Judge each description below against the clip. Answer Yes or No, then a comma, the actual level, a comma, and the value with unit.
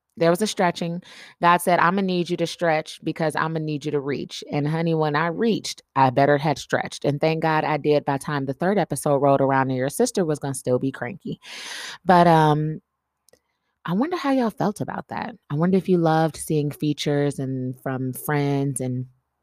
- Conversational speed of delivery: No, fast, 215 wpm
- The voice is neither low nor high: Yes, medium, 155 Hz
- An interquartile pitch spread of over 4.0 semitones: No, average, 3.7 semitones